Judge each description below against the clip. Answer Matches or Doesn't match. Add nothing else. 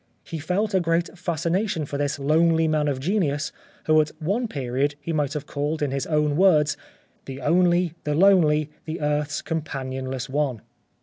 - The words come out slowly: Doesn't match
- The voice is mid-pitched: Matches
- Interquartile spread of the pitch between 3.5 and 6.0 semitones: Doesn't match